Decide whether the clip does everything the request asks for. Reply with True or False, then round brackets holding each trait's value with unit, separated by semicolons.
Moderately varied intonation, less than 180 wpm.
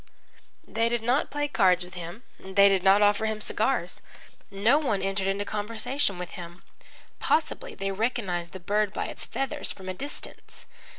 True (3.4 semitones; 170 wpm)